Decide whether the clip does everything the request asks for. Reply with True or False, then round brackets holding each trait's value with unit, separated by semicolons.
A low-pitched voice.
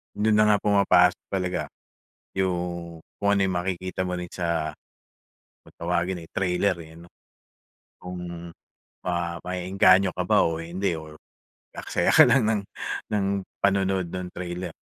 True (90 Hz)